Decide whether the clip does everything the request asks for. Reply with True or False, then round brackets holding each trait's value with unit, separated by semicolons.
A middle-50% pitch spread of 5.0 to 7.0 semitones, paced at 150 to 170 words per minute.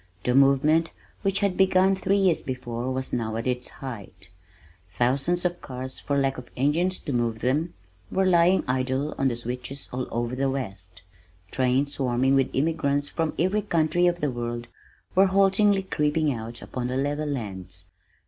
True (5.3 semitones; 165 wpm)